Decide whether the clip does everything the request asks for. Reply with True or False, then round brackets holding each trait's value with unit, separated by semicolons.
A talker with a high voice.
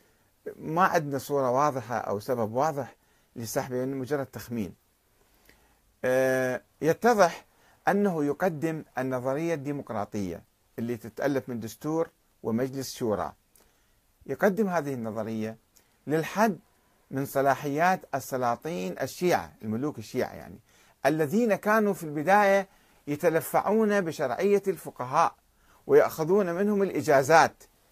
False (145 Hz)